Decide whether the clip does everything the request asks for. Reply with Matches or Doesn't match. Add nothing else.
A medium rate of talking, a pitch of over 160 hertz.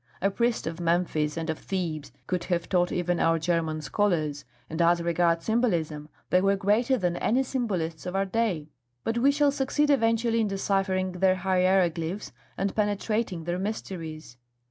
Matches